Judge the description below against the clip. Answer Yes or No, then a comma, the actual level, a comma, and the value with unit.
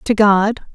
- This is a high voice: Yes, high, 210 Hz